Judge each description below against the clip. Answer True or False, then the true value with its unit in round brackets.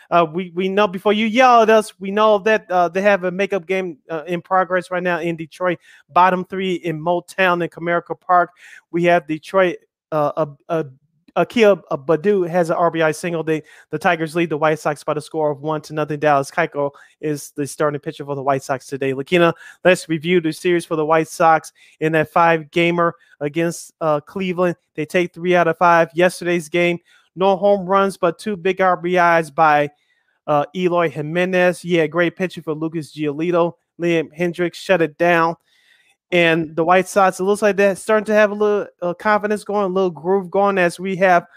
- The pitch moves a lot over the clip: False (2.6 semitones)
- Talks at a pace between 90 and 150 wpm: False (200 wpm)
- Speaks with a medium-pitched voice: True (175 Hz)